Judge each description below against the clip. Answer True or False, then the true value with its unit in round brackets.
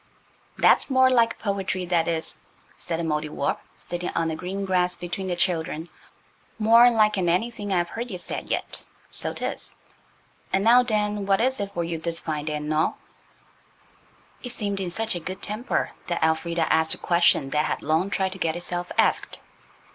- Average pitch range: True (3.9 semitones)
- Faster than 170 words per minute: True (180 wpm)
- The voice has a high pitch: False (180 Hz)